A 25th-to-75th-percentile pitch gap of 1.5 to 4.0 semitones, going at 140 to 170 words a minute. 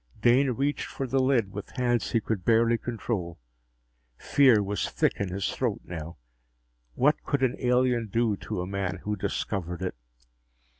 No: average, 4.4 semitones; average, 160 wpm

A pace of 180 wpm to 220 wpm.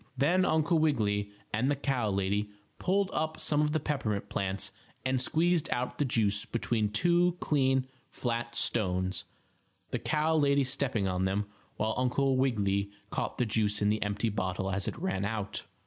No: average, 165 wpm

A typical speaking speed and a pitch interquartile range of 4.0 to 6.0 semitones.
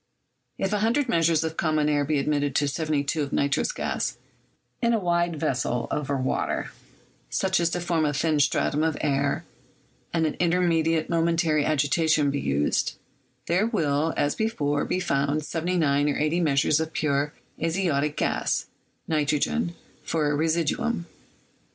No: average, 145 wpm; average, 2.8 semitones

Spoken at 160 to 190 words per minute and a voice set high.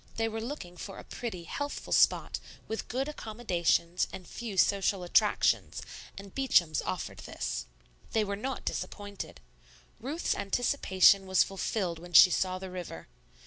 No: average, 145 wpm; high, 195 Hz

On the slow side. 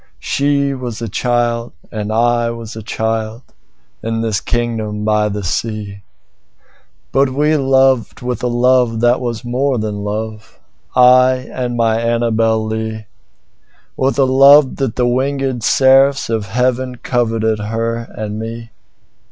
Yes: slow, 120 wpm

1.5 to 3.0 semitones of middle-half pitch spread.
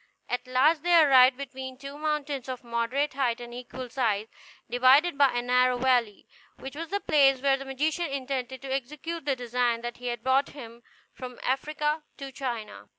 Yes: narrow, 2.4 semitones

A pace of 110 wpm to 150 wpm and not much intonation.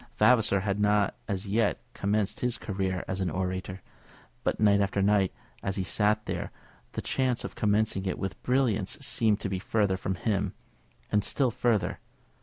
No: average, 170 wpm; narrow, 2.2 semitones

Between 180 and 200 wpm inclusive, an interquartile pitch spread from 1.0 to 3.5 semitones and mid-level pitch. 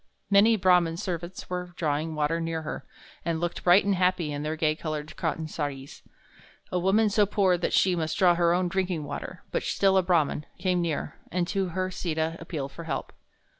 Yes: average, 195 wpm; average, 2.7 semitones; medium, 175 Hz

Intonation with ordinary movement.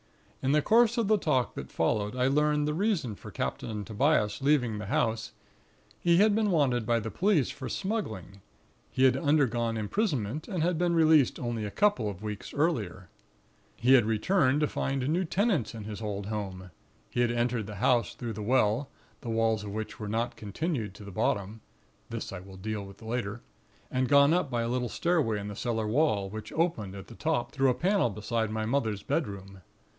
No: wide, 6.0 semitones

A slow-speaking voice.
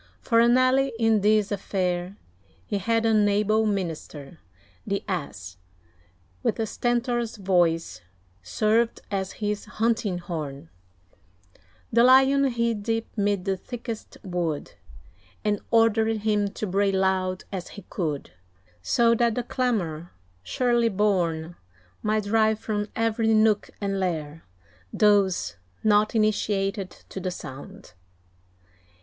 Yes: slow, 120 wpm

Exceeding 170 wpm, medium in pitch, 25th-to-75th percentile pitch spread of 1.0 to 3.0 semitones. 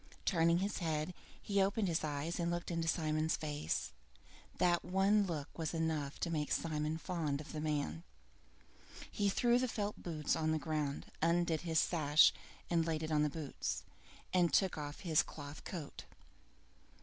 No: average, 160 wpm; medium, 160 Hz; narrow, 2.4 semitones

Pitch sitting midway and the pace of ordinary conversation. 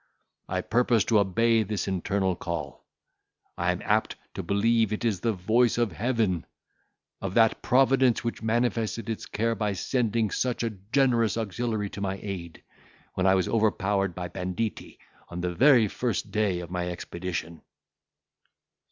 No: low, 105 Hz; average, 150 wpm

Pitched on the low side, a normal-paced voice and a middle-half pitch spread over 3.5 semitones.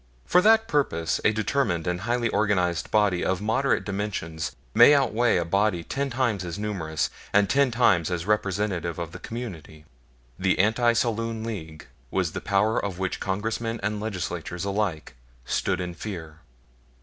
Yes: low, 100 Hz; average, 155 wpm; average, 4.4 semitones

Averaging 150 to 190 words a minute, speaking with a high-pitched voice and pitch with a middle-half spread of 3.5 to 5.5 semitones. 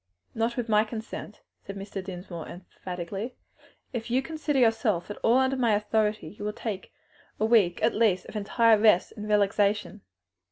No: average, 165 wpm; high, 210 Hz; narrow, 2.5 semitones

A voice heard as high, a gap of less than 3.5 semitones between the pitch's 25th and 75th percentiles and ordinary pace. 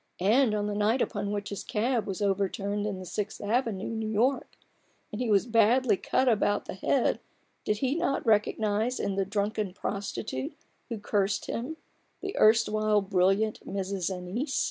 Yes: high, 210 Hz; narrow, 2.4 semitones; average, 165 wpm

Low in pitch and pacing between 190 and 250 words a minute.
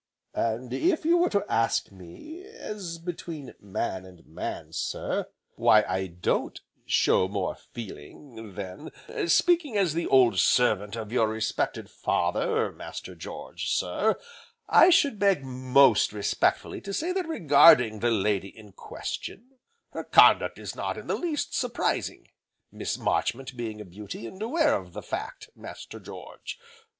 No: low, 130 Hz; average, 145 wpm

